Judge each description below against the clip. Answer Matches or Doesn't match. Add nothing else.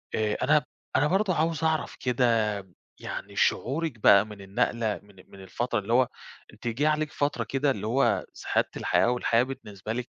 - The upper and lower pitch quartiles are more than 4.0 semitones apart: Matches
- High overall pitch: Doesn't match